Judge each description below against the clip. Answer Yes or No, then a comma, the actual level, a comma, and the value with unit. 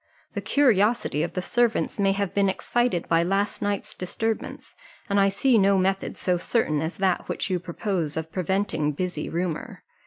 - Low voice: No, high, 195 Hz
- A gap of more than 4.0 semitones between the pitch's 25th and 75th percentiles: No, average, 2.8 semitones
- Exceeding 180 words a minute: No, average, 175 wpm